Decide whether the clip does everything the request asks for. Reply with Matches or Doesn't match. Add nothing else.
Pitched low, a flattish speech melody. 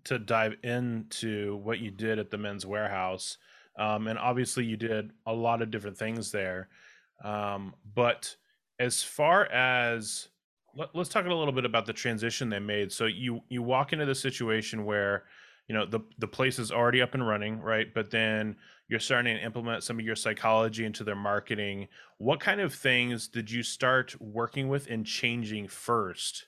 Matches